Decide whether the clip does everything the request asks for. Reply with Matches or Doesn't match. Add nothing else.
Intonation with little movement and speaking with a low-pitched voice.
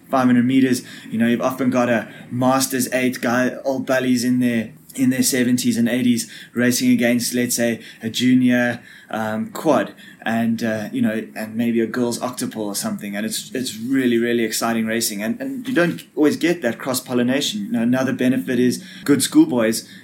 Matches